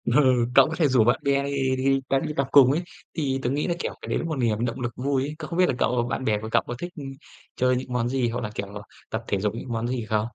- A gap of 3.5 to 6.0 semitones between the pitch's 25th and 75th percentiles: No, average, 2.8 semitones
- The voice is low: Yes, low, 130 Hz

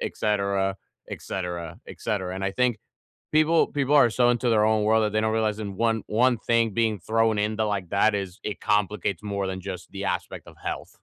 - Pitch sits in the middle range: No, low, 105 Hz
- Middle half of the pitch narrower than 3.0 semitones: Yes, narrow, 2.5 semitones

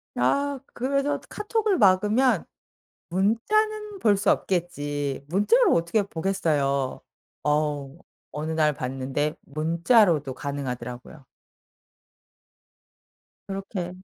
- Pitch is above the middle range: No, medium, 170 Hz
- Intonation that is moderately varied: No, wide, 7.0 semitones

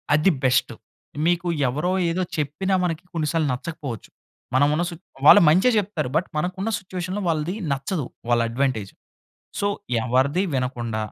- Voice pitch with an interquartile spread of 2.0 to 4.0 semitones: No, wide, 5.4 semitones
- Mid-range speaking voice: Yes, medium, 155 Hz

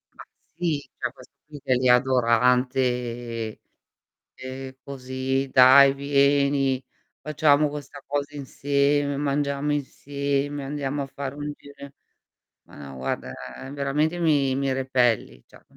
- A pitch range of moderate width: No, narrow, 1.8 semitones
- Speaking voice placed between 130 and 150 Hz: Yes, medium, 140 Hz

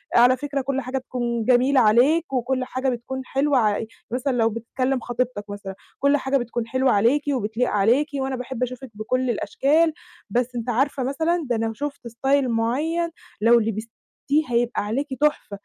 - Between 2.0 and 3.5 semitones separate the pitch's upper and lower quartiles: Yes, average, 2.8 semitones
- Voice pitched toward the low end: No, very high, 250 Hz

